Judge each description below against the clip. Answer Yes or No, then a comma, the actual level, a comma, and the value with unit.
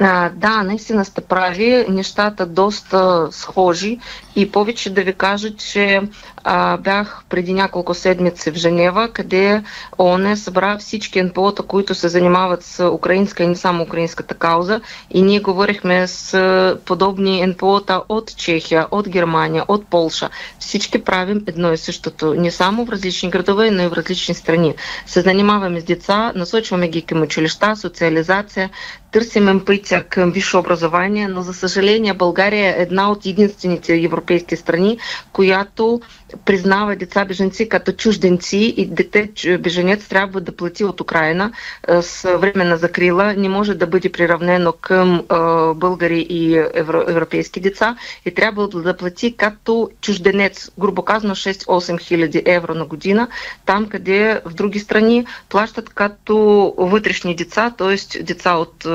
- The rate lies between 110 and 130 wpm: No, average, 145 wpm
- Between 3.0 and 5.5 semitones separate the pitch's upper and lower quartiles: No, narrow, 2.6 semitones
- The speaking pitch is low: No, high, 190 Hz